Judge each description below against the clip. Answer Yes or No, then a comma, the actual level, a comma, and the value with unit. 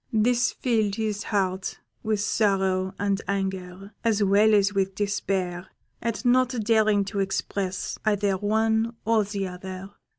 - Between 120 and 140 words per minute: Yes, slow, 135 wpm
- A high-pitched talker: Yes, high, 200 Hz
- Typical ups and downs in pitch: No, narrow, 2.2 semitones